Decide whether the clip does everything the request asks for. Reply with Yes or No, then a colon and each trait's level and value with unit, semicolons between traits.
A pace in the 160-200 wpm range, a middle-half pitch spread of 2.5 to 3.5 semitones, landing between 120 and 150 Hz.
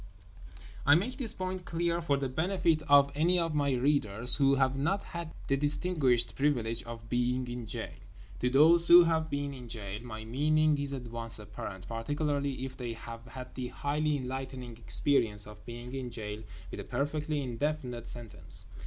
No: average, 175 wpm; average, 4.2 semitones; low, 135 Hz